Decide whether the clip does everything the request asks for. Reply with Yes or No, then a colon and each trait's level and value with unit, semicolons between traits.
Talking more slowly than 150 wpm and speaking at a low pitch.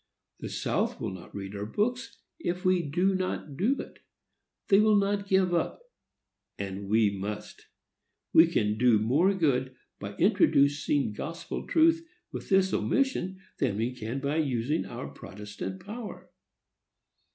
No: average, 140 wpm; medium, 145 Hz